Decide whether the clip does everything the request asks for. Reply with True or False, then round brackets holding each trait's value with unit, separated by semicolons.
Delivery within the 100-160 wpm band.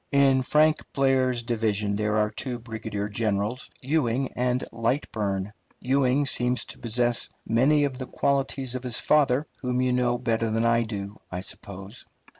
True (155 wpm)